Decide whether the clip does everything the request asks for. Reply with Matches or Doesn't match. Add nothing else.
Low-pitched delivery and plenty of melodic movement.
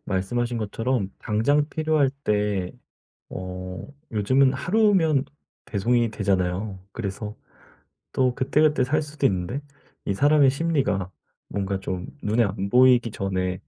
Matches